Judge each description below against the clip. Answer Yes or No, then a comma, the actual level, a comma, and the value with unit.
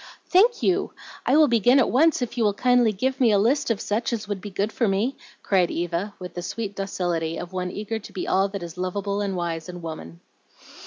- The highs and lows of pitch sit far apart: No, average, 4.8 semitones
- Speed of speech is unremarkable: No, fast, 230 wpm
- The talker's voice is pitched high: Yes, high, 200 Hz